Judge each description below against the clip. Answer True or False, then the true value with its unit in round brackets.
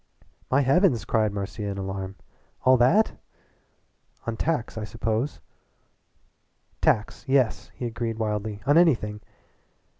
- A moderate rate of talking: False (115 wpm)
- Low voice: True (115 Hz)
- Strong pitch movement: False (3.7 semitones)